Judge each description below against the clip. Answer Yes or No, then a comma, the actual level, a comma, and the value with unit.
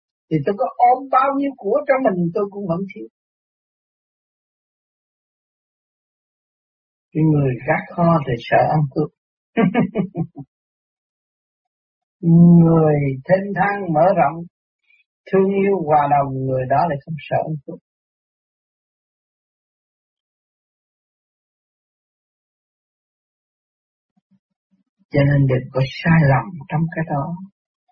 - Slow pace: Yes, slow, 95 wpm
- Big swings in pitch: No, average, 5.0 semitones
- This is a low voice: No, medium, 170 Hz